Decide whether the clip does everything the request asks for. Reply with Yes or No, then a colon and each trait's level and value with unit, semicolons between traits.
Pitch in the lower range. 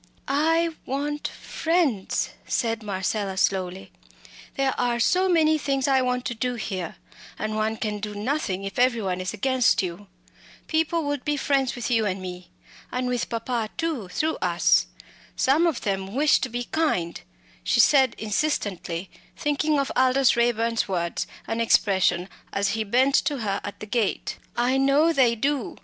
No: high, 240 Hz